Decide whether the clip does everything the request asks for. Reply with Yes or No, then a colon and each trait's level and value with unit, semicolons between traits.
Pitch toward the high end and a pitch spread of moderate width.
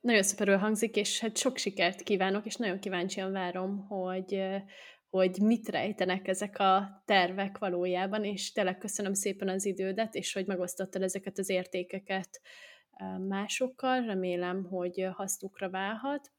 No: high, 195 Hz; narrow, 1.6 semitones